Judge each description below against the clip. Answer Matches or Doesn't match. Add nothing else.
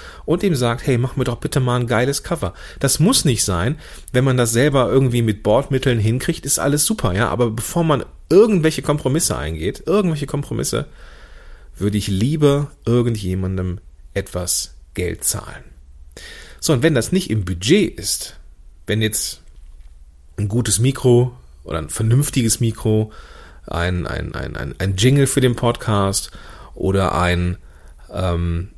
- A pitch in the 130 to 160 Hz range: Doesn't match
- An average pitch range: Doesn't match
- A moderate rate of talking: Matches